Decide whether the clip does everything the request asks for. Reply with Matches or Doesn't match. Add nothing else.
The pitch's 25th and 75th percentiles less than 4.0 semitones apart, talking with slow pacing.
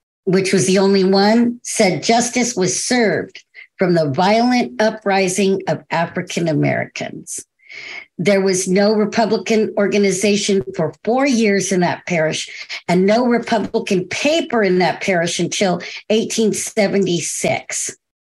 Matches